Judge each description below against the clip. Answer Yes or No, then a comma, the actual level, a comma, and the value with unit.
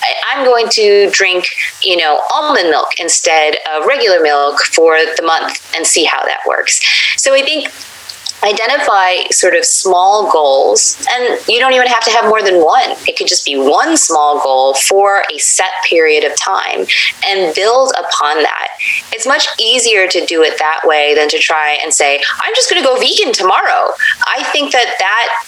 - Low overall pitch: No, high, 230 Hz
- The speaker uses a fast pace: No, average, 185 wpm